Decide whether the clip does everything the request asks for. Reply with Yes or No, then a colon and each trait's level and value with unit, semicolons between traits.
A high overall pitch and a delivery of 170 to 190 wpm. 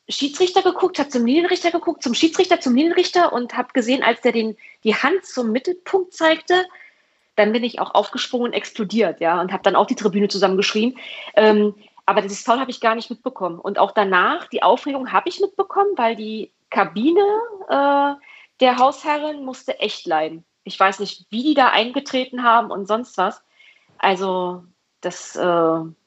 Yes: high, 240 Hz; average, 175 wpm